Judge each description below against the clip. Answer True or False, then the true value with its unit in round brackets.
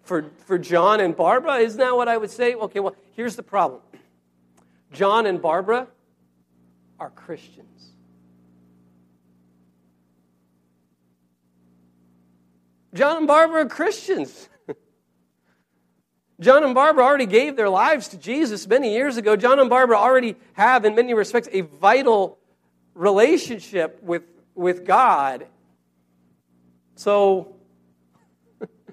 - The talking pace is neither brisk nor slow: False (110 wpm)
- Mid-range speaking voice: True (170 Hz)